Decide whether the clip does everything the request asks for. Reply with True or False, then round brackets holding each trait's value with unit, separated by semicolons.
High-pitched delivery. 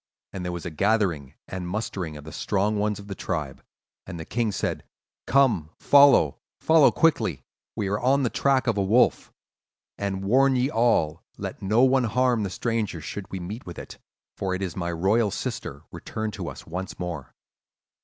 False (100 Hz)